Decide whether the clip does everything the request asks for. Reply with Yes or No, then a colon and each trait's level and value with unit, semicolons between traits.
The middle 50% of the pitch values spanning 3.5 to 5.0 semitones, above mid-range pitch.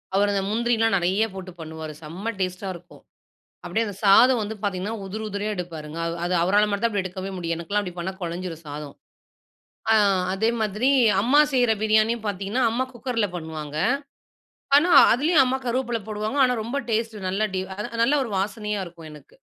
Yes: average, 4.1 semitones; high, 205 Hz